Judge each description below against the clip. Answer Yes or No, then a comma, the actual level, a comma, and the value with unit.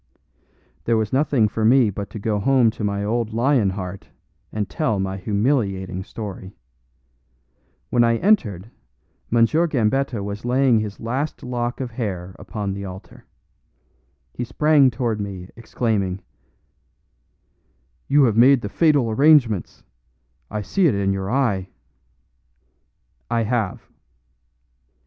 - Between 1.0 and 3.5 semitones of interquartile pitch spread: No, average, 4.2 semitones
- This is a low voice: Yes, low, 110 Hz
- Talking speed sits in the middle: No, slow, 125 wpm